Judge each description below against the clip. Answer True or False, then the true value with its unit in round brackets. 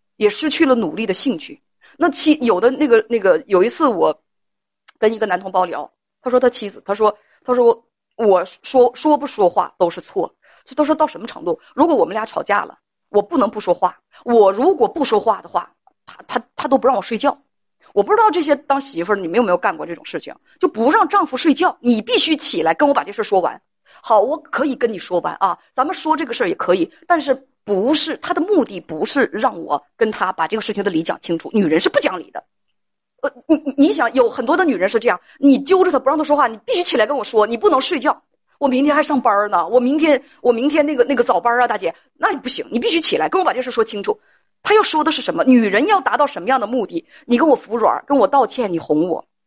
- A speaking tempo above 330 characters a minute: True (340 characters per minute)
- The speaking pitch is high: True (260 Hz)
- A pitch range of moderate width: False (6.4 semitones)